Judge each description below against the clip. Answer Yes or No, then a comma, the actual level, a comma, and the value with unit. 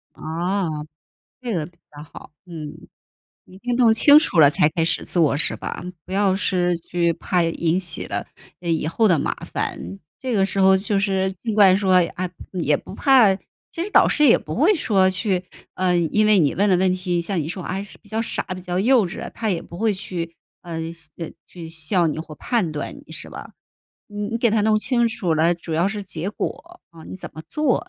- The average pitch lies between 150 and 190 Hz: Yes, medium, 185 Hz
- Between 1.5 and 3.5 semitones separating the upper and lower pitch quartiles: No, average, 4.1 semitones